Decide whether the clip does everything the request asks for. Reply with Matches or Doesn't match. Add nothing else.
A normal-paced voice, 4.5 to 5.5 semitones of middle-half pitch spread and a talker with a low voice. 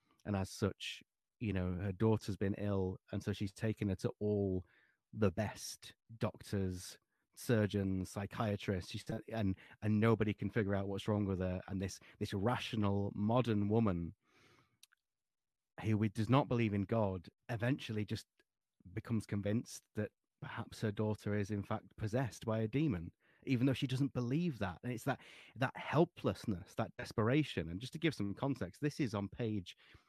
Doesn't match